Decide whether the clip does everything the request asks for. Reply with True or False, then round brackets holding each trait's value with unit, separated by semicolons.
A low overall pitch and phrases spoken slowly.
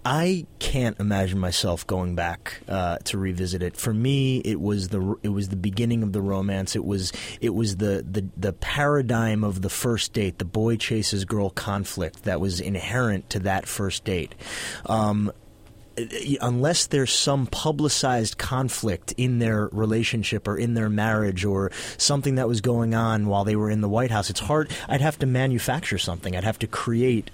False (105 Hz; 185 wpm)